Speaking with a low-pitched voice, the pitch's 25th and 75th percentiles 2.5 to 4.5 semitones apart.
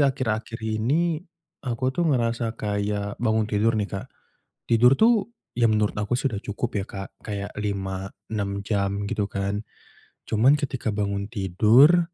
Yes: low, 110 Hz; average, 3.2 semitones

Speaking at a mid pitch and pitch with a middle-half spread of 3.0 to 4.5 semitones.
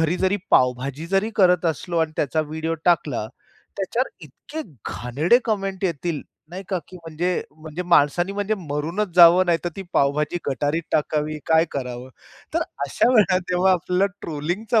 Yes: medium, 170 Hz; average, 3.8 semitones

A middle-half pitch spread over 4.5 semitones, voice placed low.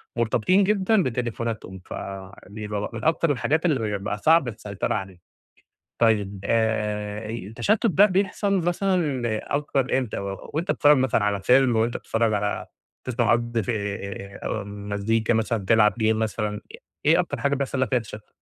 Yes: average, 5.3 semitones; low, 115 Hz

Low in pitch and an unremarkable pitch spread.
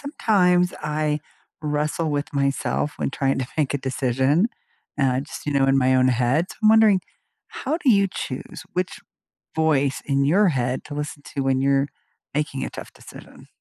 No: medium, 145 Hz; average, 3.8 semitones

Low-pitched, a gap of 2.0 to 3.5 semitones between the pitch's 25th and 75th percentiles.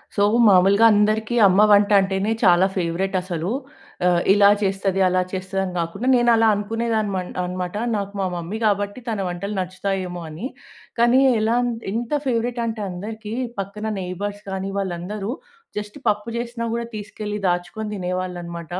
No: high, 200 Hz; average, 2.9 semitones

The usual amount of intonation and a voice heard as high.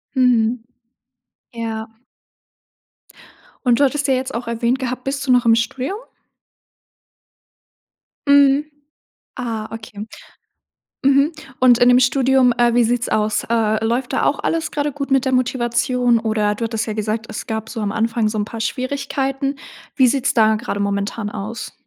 Yes: average, 3.1 semitones; high, 240 Hz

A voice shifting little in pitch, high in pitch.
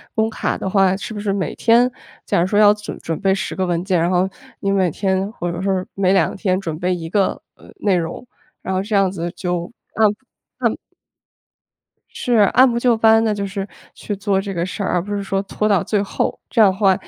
Yes: narrow, 2.3 semitones; high, 195 Hz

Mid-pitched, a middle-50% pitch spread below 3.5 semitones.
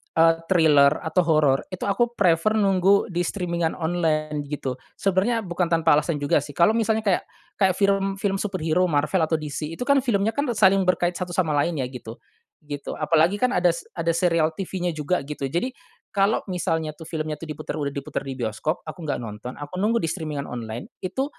No: medium, 170 Hz; average, 4.2 semitones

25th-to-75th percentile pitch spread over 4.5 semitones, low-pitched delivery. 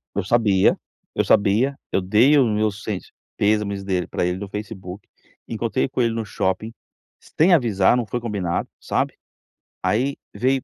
No: average, 3.4 semitones; low, 105 Hz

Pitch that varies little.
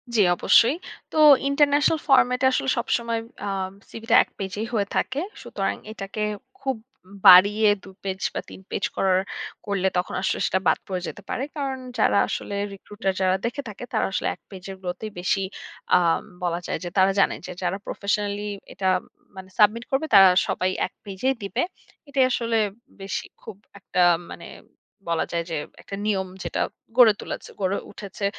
No: average, 3.7 semitones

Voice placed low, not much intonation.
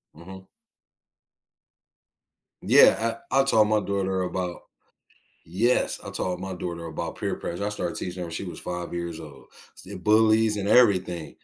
No: very low, 95 Hz; average, 3.5 semitones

